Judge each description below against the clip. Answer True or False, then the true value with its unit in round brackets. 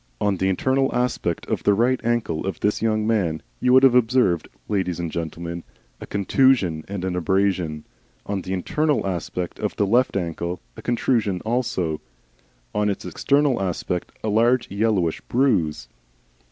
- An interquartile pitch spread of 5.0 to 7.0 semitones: True (5.4 semitones)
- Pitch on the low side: True (100 Hz)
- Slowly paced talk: False (155 wpm)